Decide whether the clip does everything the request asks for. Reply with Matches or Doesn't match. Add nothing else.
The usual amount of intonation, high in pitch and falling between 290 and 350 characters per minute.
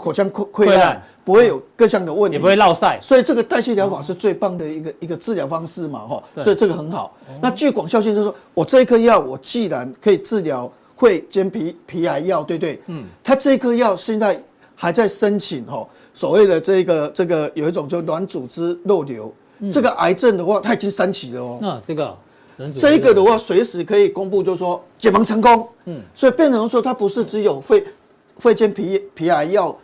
Matches